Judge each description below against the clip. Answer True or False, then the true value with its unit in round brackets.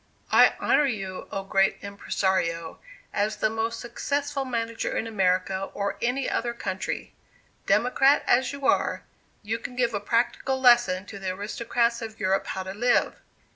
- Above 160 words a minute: False (155 wpm)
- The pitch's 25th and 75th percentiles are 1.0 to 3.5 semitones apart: False (3.9 semitones)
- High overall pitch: True (225 Hz)